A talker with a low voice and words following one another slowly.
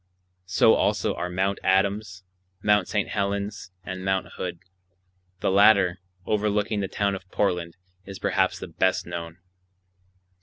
Yes: very low, 95 Hz; slow, 130 wpm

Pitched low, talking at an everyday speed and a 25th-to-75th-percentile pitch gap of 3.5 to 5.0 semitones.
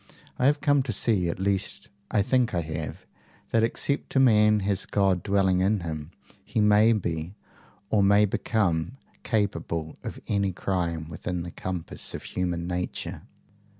Yes: very low, 95 Hz; average, 155 wpm; average, 3.8 semitones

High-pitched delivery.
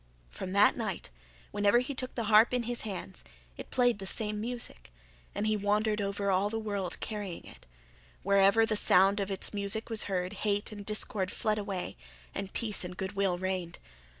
Yes: high, 205 Hz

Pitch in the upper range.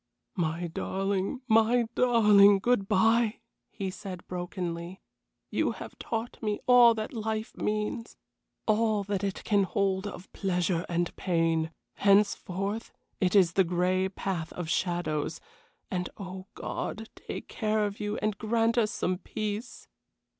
Yes: high, 200 Hz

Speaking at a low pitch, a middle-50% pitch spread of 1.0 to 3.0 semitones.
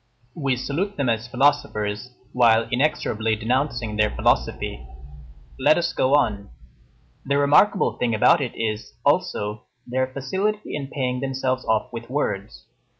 No: low, 125 Hz; average, 4.2 semitones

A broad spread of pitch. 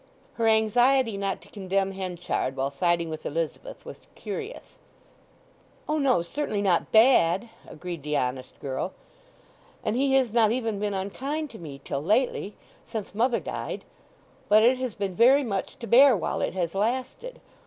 Yes: wide, 6.1 semitones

